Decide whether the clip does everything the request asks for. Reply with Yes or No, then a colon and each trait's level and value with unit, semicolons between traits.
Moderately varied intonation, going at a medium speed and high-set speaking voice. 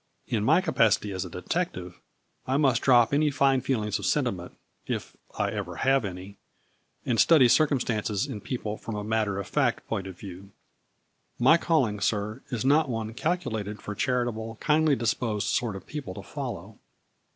No: average, 4.7 semitones; average, 175 wpm; low, 115 Hz